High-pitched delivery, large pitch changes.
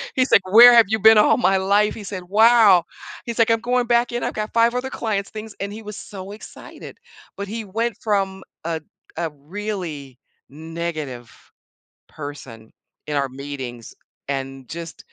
Yes: high, 195 Hz; wide, 6.6 semitones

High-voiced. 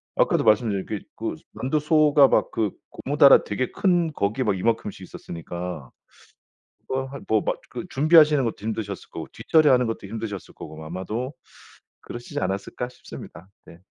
No: low, 115 Hz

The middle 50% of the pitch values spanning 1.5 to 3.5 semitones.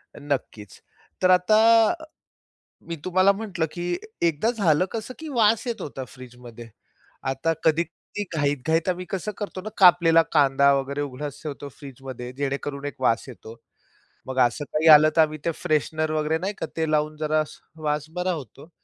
No: average, 4.4 semitones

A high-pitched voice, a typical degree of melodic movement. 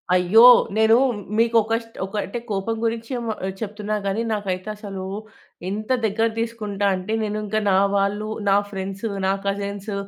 No: high, 210 Hz; narrow, 2.0 semitones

